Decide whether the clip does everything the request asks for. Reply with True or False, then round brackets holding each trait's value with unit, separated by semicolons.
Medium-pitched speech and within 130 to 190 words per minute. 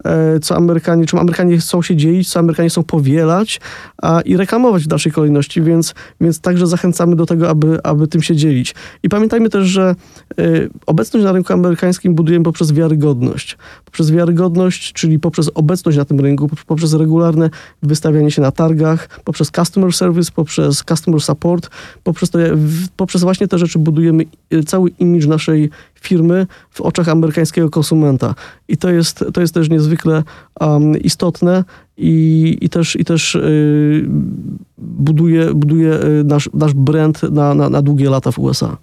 True (165 Hz; 160 wpm)